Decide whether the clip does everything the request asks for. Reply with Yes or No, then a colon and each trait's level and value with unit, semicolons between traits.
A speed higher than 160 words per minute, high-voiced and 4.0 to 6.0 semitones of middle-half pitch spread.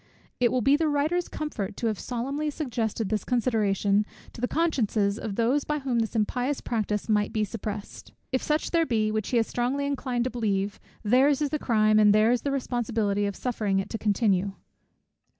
Yes: average, 190 wpm; high, 230 Hz; average, 4.3 semitones